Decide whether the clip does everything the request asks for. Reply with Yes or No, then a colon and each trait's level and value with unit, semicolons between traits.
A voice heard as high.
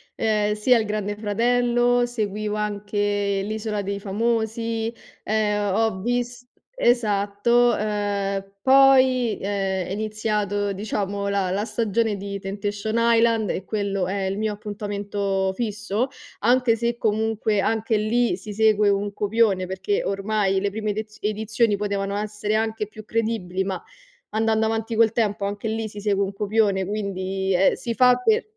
Yes: high, 210 Hz